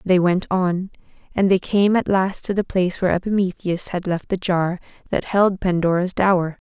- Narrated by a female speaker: Yes, female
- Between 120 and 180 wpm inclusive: No, average, 190 wpm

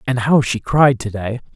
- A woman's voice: No, male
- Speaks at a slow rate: No, fast, 230 wpm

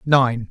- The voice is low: Yes, low, 125 Hz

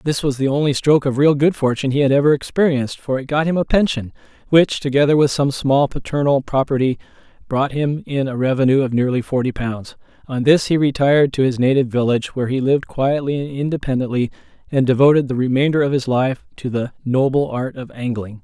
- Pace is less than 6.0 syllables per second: No, 6.1 syllables/s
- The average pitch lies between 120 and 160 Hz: Yes, low, 135 Hz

